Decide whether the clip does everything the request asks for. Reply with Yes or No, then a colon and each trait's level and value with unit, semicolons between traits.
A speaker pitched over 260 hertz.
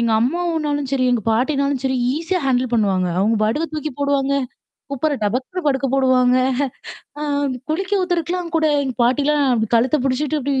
Yes: very high, 275 Hz